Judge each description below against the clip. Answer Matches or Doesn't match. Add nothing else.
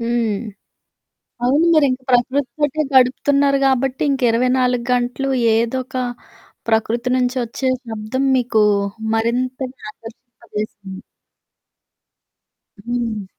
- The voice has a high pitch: Matches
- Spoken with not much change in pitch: Matches